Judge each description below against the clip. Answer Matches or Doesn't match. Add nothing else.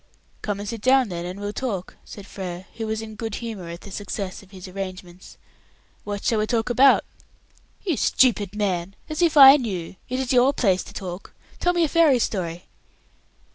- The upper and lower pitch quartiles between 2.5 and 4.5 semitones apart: Doesn't match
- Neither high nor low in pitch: Doesn't match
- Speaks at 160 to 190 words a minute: Matches